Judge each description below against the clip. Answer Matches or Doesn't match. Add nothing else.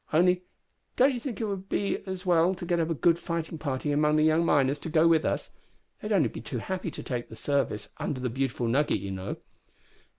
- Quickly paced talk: Matches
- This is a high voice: Doesn't match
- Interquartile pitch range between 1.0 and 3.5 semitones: Doesn't match